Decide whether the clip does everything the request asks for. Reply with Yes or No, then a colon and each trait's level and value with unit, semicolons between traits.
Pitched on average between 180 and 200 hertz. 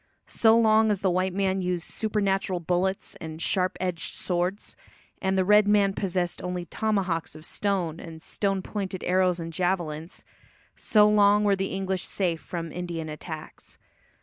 Yes: medium, 185 Hz